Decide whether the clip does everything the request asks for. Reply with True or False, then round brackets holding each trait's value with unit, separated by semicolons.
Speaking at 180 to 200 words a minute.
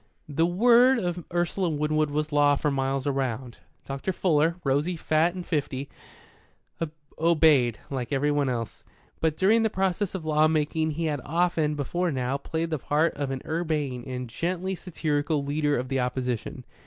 False (160 wpm)